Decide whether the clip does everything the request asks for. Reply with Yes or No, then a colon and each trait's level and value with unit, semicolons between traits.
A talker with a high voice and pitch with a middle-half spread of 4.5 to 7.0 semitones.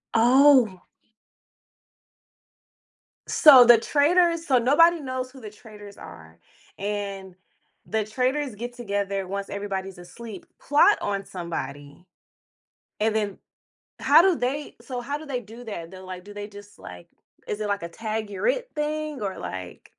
Yes: high, 215 Hz; average, 5.2 semitones